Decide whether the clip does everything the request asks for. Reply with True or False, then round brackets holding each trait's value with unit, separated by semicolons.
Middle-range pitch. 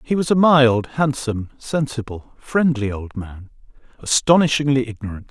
False (130 Hz)